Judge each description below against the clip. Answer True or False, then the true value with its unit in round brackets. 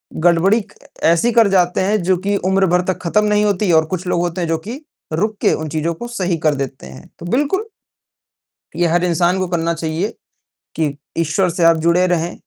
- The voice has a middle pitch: True (175 Hz)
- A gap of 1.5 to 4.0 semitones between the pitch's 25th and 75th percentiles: True (2.9 semitones)